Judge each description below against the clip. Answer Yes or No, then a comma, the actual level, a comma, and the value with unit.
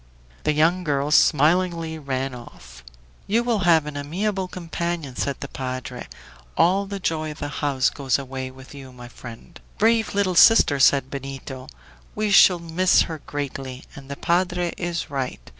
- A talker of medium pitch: Yes, medium, 150 Hz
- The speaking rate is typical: Yes, average, 160 wpm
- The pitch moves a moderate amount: Yes, average, 4.8 semitones